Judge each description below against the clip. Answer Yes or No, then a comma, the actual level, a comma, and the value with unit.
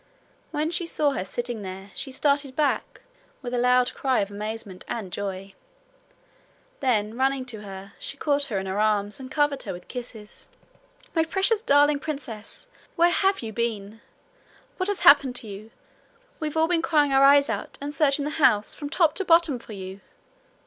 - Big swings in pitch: Yes, wide, 5.9 semitones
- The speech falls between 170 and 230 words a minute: Yes, average, 180 wpm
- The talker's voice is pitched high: Yes, very high, 260 Hz